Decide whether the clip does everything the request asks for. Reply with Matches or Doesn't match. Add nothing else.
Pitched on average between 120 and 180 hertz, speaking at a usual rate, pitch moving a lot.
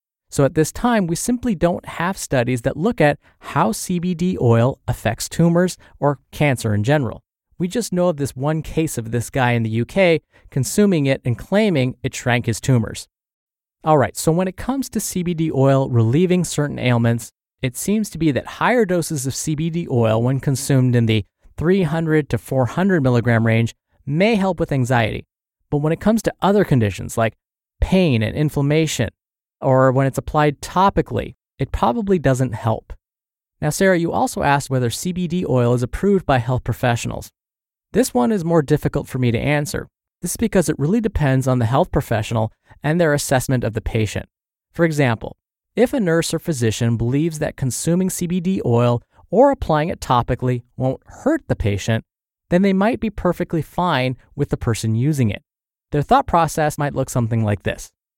Matches